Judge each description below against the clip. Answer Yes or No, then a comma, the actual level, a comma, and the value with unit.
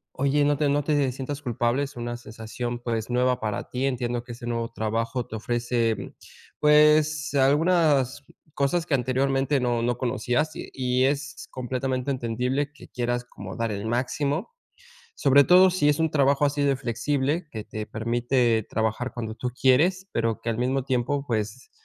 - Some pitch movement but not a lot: Yes, average, 3.2 semitones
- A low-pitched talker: Yes, low, 130 Hz